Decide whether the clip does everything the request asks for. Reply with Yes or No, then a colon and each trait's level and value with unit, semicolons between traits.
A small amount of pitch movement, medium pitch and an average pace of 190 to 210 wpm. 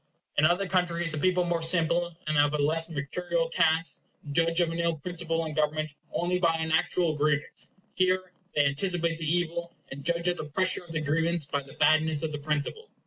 Yes: narrow, 2.2 semitones; medium, 165 Hz; average, 200 wpm